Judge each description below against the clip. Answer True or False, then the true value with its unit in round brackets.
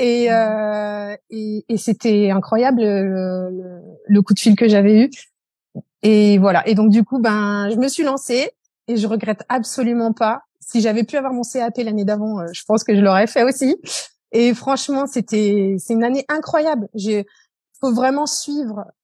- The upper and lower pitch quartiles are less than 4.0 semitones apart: True (3.1 semitones)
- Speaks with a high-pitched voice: True (220 Hz)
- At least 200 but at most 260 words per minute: False (180 wpm)